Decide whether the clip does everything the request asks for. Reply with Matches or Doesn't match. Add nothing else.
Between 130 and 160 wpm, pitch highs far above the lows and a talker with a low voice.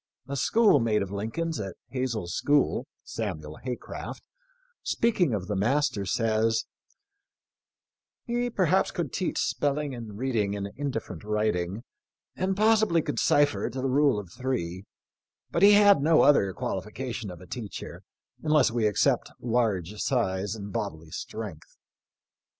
Matches